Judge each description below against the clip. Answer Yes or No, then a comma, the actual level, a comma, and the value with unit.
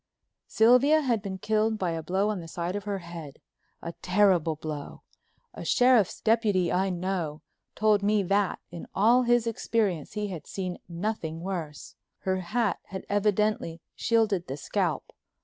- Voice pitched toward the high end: Yes, high, 195 Hz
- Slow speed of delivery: No, average, 150 wpm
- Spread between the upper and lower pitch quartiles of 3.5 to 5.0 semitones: Yes, average, 3.9 semitones